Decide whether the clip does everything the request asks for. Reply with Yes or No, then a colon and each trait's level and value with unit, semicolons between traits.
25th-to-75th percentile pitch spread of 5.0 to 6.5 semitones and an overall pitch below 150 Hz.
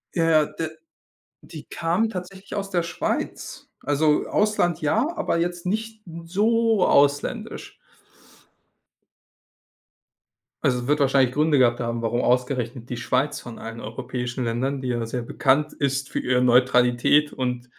Yes: wide, 5.5 semitones; medium, 140 Hz